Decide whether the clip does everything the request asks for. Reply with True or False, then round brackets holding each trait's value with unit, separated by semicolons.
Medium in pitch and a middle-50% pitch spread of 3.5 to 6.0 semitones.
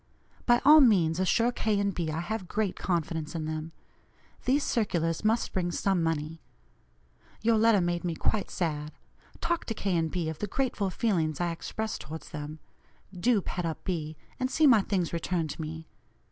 True (175 Hz; 5.2 semitones)